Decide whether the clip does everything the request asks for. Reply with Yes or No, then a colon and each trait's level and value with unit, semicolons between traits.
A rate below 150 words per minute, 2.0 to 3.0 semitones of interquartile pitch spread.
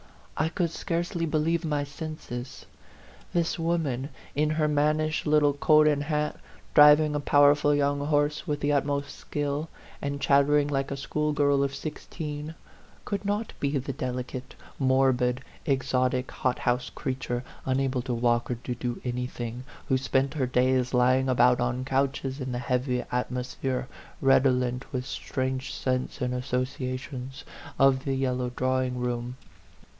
Yes: average, 140 wpm; average, 2.7 semitones